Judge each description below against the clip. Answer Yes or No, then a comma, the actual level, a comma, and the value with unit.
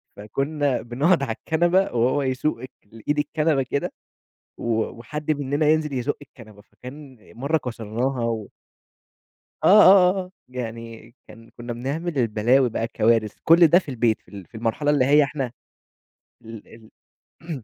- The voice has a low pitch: Yes, low, 130 Hz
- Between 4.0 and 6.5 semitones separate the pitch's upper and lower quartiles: Yes, average, 4.7 semitones